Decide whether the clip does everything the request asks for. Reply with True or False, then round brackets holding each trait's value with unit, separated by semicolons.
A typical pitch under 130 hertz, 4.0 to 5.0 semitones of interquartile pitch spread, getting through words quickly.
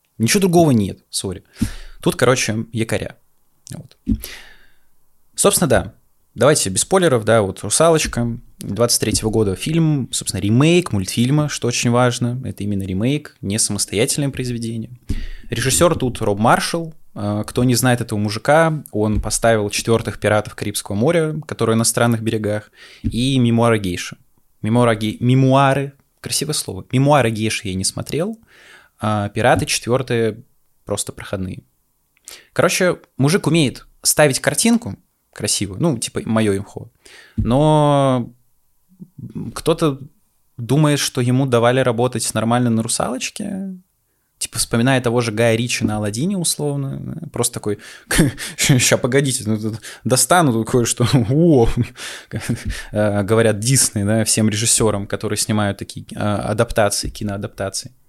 False (120 Hz; 4.3 semitones; 120 wpm)